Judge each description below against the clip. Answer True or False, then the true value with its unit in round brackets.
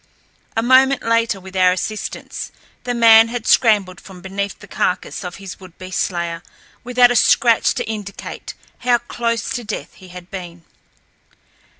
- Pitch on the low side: False (205 Hz)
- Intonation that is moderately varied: True (4.1 semitones)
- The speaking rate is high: False (160 wpm)